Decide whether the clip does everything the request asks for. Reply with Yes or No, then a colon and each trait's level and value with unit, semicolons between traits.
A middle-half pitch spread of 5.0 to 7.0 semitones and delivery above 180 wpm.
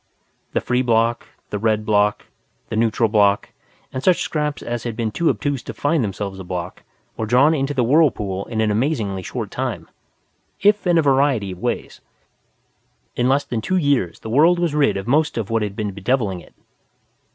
Yes: wide, 5.6 semitones; average, 190 wpm